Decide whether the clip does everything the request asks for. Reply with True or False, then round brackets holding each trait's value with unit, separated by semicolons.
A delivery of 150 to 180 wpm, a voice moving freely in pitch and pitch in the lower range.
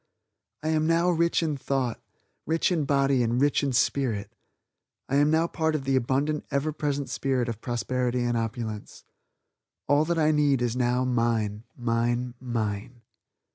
False (160 wpm; 3.8 semitones; 130 Hz)